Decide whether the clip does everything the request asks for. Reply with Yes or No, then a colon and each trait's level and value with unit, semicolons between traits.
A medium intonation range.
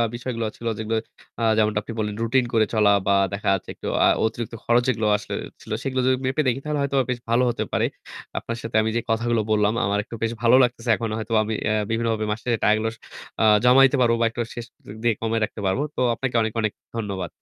No: narrow, 1.9 semitones